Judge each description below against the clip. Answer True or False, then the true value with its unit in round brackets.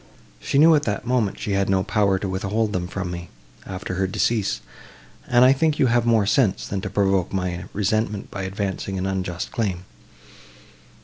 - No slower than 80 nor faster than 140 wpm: False (185 wpm)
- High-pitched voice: False (100 Hz)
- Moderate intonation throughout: True (3.1 semitones)